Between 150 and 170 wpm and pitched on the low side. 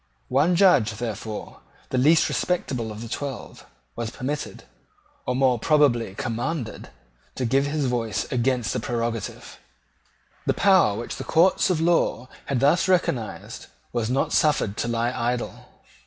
No: average, 140 wpm; low, 125 Hz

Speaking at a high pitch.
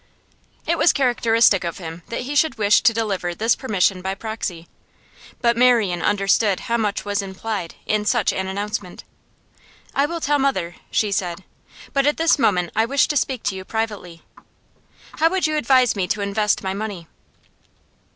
Yes: high, 215 Hz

